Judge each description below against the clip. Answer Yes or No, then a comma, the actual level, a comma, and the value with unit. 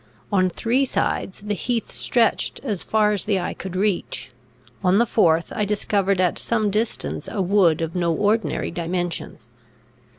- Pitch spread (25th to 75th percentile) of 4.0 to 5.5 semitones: No, average, 3.3 semitones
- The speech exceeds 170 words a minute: No, average, 160 wpm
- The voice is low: No, high, 195 Hz